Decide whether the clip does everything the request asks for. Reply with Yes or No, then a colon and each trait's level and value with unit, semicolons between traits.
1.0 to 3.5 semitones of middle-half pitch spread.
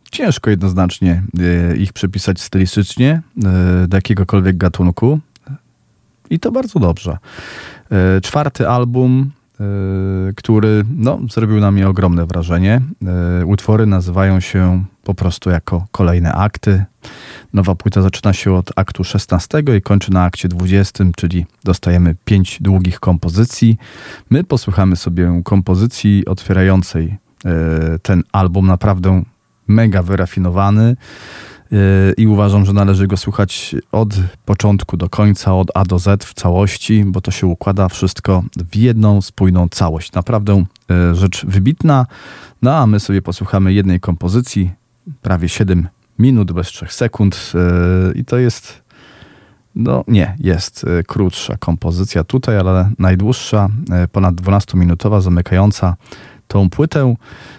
Yes: average, 2.9 semitones